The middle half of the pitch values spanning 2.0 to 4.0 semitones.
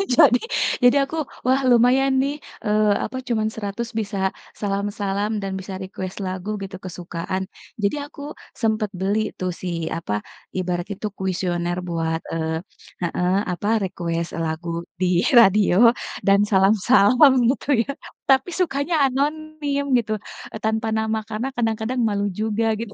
No: average, 4.7 semitones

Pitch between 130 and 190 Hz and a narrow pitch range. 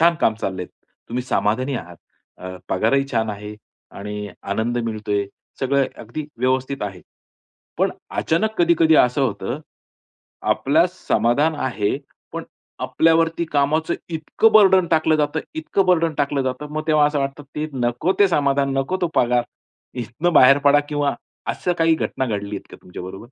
No: medium, 140 Hz; wide, 5.6 semitones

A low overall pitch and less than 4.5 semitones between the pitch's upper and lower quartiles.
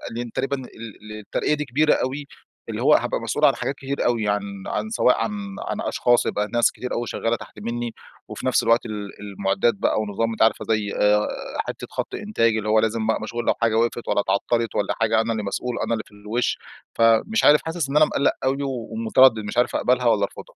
Yes: low, 115 Hz; average, 2.8 semitones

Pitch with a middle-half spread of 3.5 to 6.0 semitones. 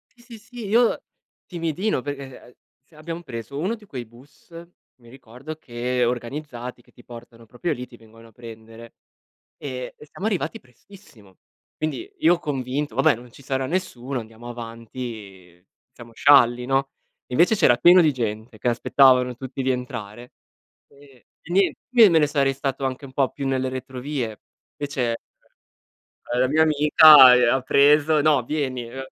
Yes: average, 3.9 semitones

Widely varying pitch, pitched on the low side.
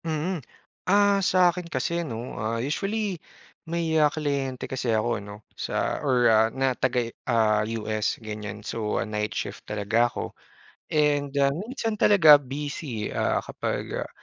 Yes: wide, 6.6 semitones; low, 130 Hz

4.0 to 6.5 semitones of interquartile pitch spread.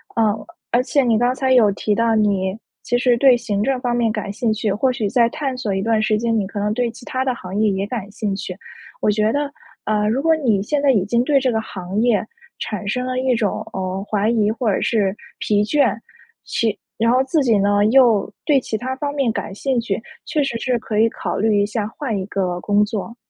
No: average, 3.5 semitones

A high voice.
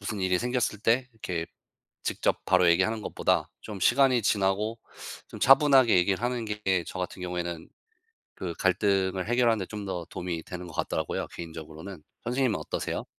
No: very low, 95 Hz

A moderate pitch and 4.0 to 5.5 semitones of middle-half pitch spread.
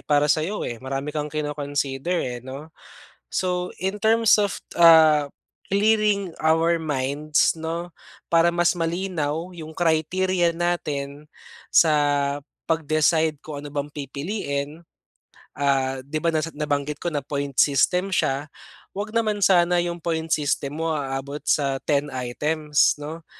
No: medium, 155 Hz; average, 3.3 semitones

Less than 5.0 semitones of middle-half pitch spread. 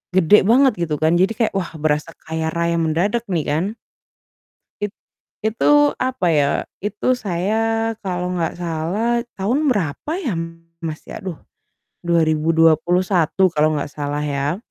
No: average, 5.3 semitones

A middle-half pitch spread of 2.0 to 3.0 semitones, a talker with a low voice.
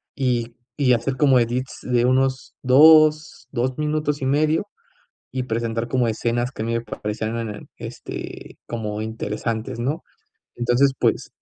Yes: average, 2.7 semitones; low, 125 Hz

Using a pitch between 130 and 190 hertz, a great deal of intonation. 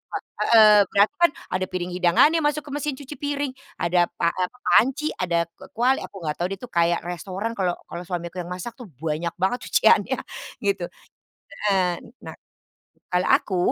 Yes: medium, 185 Hz; wide, 6.1 semitones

